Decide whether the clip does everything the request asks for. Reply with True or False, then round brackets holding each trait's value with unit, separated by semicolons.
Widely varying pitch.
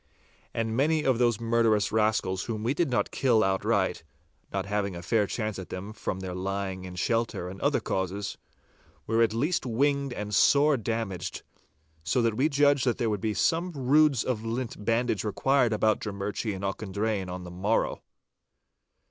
False (4.0 semitones)